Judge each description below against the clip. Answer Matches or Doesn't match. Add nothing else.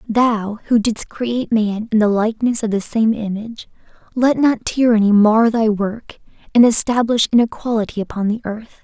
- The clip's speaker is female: Matches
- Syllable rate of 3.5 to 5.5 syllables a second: Matches